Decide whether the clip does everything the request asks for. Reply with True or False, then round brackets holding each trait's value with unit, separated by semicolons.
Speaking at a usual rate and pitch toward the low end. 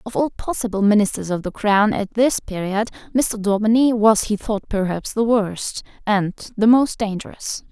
False (170 wpm; 210 Hz)